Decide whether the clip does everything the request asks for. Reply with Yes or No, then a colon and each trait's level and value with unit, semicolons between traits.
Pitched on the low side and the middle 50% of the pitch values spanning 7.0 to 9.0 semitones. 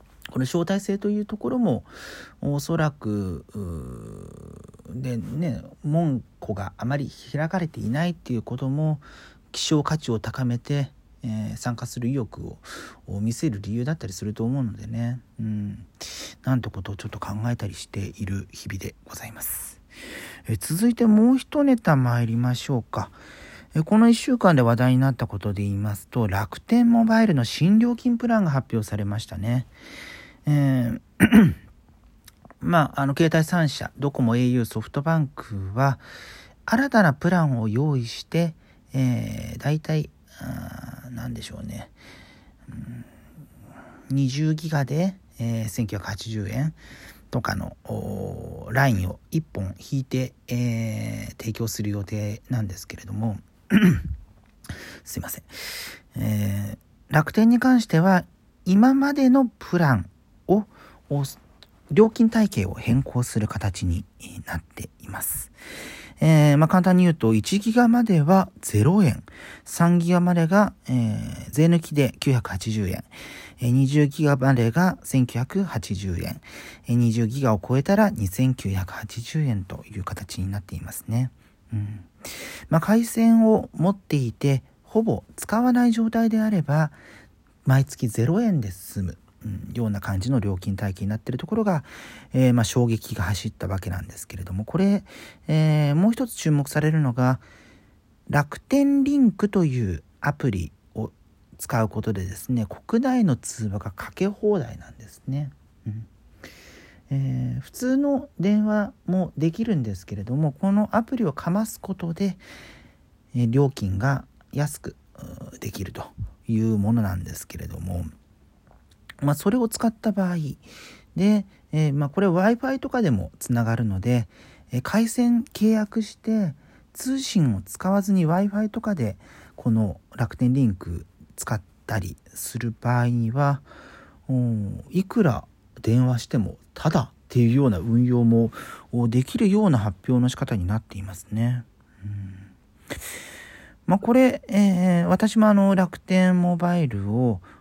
Yes: low, 125 Hz; wide, 8.3 semitones